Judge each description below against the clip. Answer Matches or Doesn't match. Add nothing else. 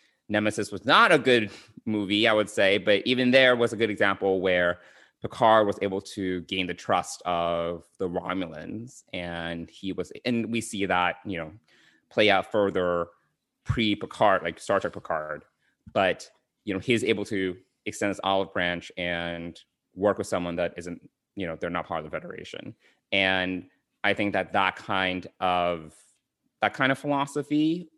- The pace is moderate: Matches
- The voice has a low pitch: Matches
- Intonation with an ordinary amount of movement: Matches